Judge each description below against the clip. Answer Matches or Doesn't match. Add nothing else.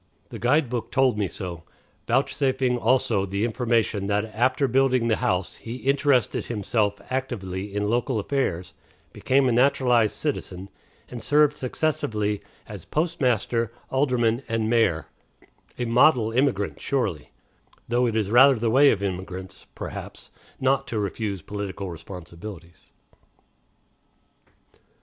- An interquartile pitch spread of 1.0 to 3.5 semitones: Doesn't match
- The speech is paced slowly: Matches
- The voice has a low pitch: Matches